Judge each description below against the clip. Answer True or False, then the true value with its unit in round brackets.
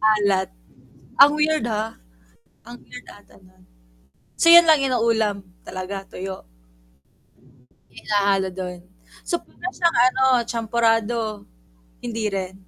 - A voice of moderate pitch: False (220 Hz)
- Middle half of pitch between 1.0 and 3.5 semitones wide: False (4.3 semitones)